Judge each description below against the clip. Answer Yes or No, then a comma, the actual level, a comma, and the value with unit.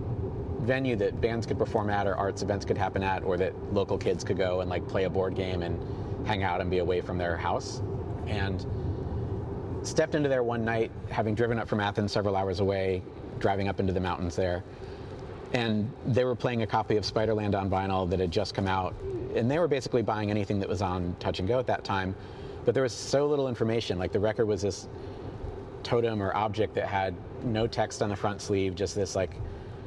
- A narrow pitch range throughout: No, average, 3.1 semitones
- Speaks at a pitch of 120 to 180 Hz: No, low, 100 Hz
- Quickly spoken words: Yes, fast, 215 wpm